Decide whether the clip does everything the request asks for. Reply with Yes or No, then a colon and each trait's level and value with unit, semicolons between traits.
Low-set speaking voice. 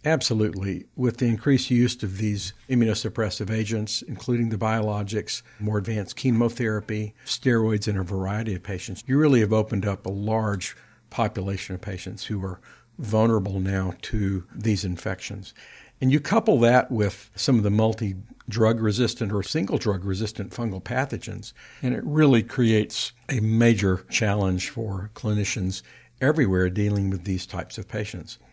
Yes: low, 110 Hz